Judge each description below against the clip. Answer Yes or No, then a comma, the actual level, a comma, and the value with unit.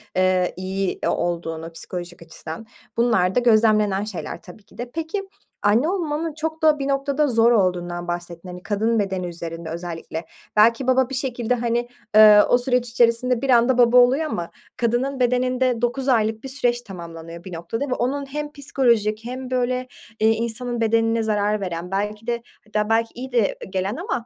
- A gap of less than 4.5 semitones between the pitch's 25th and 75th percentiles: No, average, 5.1 semitones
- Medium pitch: No, high, 230 Hz